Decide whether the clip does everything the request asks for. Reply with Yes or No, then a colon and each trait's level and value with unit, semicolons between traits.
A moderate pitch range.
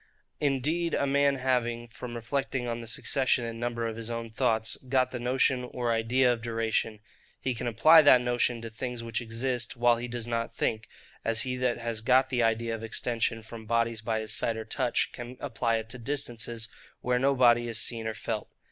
No: narrow, 1.8 semitones